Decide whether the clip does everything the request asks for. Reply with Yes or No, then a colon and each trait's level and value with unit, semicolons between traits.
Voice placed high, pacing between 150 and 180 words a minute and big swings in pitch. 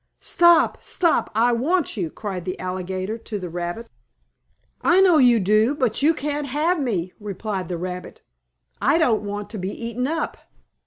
Yes: high, 225 Hz; average, 165 wpm; wide, 7.6 semitones